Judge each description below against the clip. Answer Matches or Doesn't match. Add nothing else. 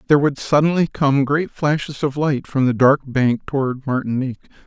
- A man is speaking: Matches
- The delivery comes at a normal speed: Matches